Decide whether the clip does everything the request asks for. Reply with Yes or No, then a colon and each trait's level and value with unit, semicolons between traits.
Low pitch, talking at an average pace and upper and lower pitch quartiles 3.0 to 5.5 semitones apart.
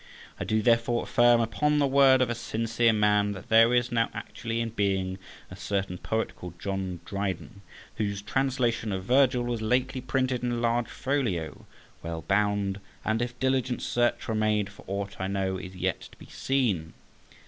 Yes: low, 115 Hz; average, 175 wpm; average, 3.6 semitones